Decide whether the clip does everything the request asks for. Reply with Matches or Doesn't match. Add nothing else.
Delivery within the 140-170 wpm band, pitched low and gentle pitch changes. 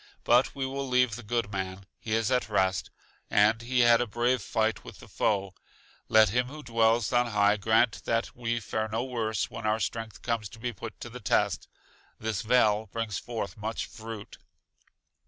Doesn't match